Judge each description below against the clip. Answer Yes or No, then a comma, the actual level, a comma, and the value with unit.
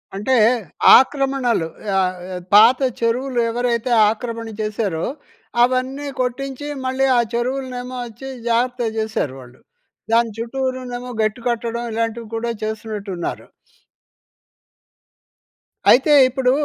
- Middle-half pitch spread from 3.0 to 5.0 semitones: No, narrow, 2.5 semitones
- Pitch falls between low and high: No, high, 240 Hz